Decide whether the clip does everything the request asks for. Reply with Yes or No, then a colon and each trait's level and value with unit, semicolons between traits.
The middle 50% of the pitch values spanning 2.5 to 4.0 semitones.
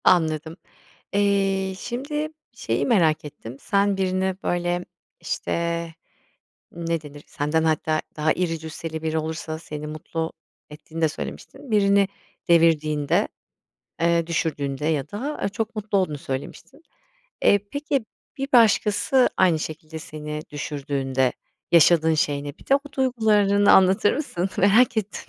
No: average, 4.7 semitones